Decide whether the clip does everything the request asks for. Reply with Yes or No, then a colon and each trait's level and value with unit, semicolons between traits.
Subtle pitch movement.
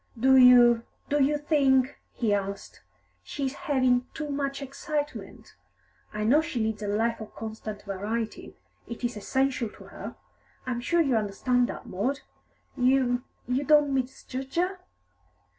No: average, 3.8 semitones